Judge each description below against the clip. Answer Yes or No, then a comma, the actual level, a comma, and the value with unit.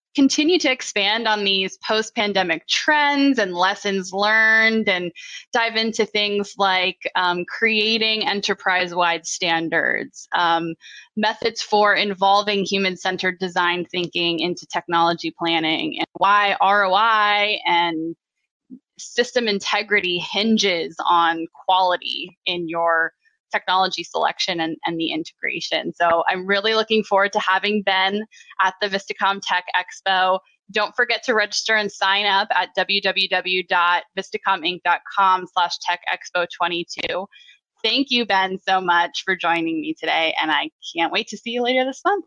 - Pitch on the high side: Yes, high, 195 Hz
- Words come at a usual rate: No, slow, 130 wpm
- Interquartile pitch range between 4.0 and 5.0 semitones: No, average, 3.6 semitones